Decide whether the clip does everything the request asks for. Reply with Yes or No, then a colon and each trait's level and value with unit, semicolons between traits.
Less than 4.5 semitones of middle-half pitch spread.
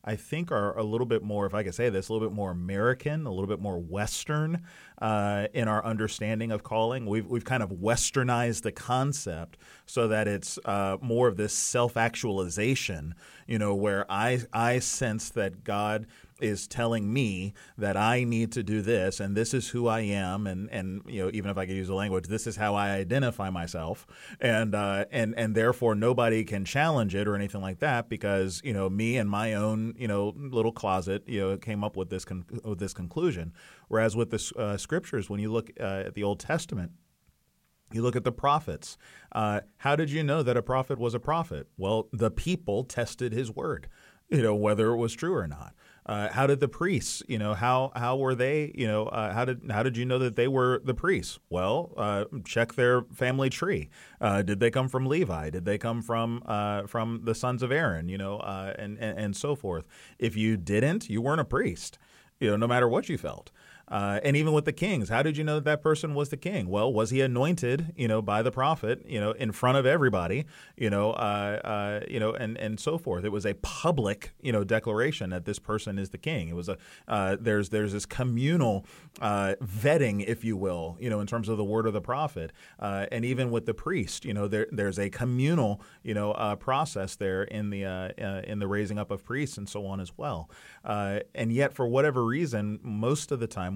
Yes: average, 3.4 semitones